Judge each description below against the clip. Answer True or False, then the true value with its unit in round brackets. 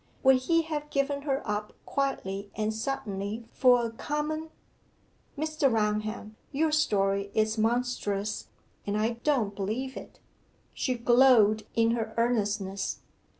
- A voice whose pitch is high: True (230 Hz)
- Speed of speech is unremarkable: False (125 wpm)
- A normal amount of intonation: True (4.5 semitones)